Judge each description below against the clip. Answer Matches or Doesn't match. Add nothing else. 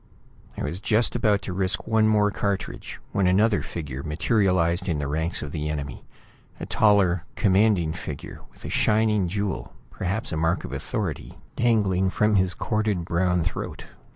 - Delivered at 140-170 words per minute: Matches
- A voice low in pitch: Matches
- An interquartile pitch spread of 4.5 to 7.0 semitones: Doesn't match